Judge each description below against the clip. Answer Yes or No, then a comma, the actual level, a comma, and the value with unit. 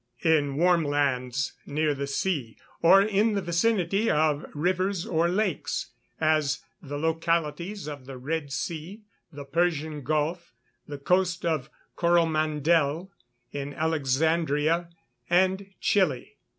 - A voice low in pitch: No, medium, 160 Hz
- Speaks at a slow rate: Yes, slow, 120 wpm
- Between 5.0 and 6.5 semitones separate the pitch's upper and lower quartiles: No, average, 3.3 semitones